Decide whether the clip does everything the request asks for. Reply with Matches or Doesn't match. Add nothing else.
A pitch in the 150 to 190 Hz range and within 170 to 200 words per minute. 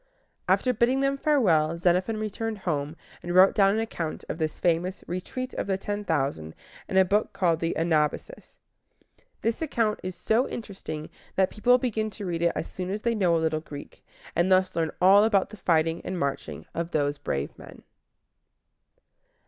Matches